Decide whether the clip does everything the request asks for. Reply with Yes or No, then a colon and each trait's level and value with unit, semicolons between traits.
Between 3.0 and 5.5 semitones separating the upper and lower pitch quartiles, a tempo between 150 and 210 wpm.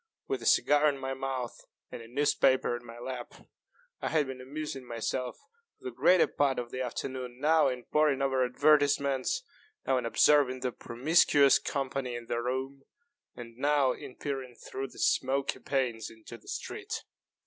No: narrow, 2.5 semitones; average, 170 wpm